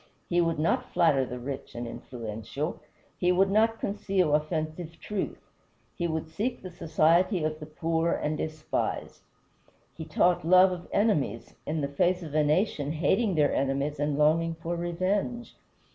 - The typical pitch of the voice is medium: Yes, medium, 165 Hz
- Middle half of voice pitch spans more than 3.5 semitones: No, average, 3.2 semitones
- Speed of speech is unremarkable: Yes, average, 160 wpm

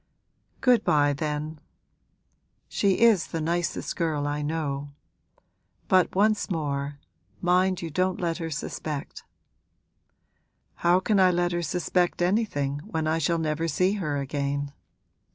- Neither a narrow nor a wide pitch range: Yes, average, 3.9 semitones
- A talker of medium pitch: Yes, medium, 165 Hz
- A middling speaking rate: No, slow, 130 wpm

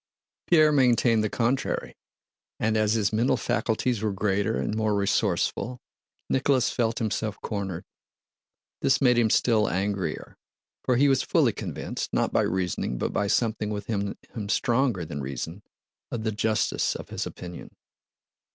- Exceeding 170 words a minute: No, average, 145 wpm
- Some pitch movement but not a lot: Yes, average, 3.1 semitones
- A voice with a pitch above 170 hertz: No, low, 110 Hz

